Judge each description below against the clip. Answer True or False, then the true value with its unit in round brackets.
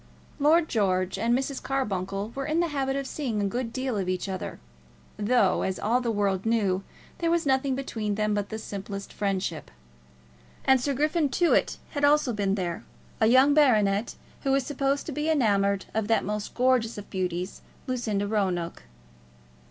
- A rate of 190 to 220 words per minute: False (175 wpm)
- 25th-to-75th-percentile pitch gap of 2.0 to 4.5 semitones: False (5.4 semitones)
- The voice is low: False (225 Hz)